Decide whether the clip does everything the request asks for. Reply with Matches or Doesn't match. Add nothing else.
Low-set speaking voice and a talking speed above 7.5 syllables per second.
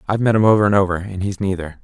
Matches